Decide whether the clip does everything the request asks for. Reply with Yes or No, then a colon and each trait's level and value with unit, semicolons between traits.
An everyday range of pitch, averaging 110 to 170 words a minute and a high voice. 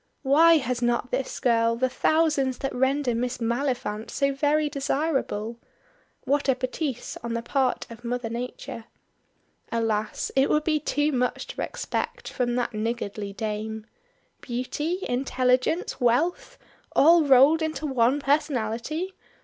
Yes: average, 3.7 semitones; slow, 135 wpm; very high, 255 Hz